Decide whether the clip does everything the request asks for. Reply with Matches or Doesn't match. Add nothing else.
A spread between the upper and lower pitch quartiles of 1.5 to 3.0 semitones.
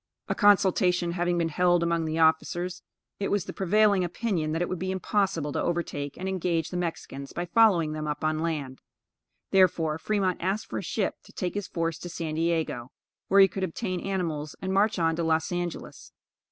Matches